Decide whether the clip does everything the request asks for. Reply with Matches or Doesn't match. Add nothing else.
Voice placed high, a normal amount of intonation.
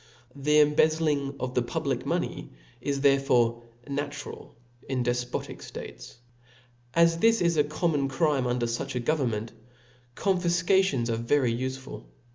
Doesn't match